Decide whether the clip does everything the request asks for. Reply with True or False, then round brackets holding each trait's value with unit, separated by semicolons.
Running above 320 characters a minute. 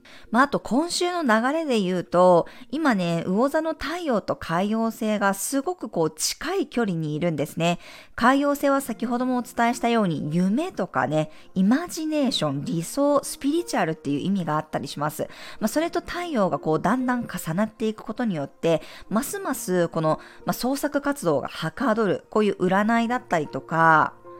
True (360 characters per minute)